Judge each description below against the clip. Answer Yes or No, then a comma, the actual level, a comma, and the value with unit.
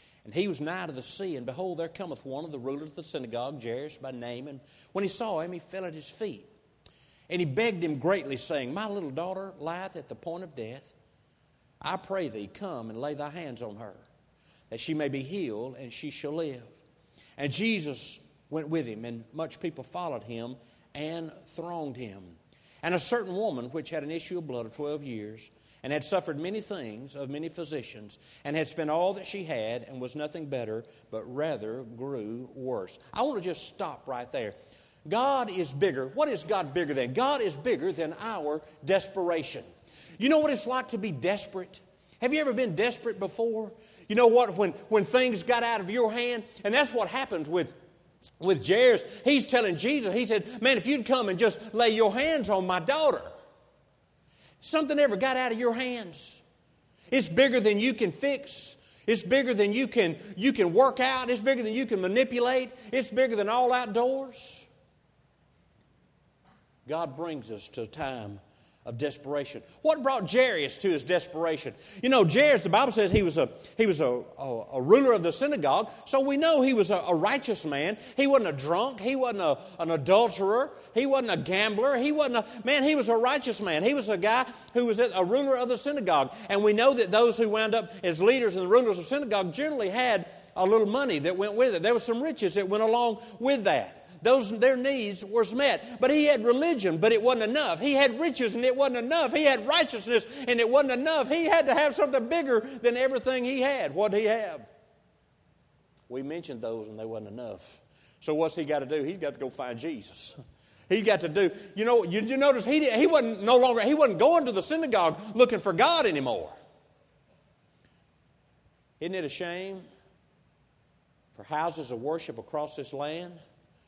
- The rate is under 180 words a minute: No, fast, 205 wpm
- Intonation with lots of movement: Yes, wide, 8.4 semitones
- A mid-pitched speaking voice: No, high, 200 Hz